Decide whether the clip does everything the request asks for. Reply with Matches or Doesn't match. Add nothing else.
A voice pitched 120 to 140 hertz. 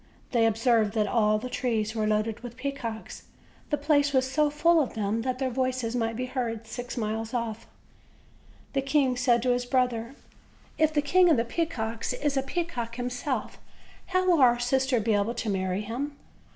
Doesn't match